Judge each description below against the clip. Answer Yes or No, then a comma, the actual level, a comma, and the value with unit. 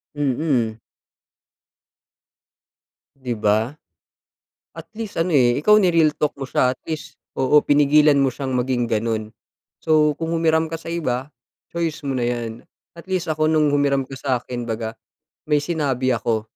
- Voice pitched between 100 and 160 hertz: Yes, medium, 140 Hz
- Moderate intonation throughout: Yes, average, 4.4 semitones